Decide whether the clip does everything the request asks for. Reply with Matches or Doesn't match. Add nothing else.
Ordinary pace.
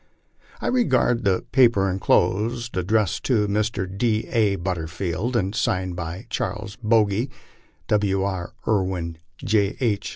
Doesn't match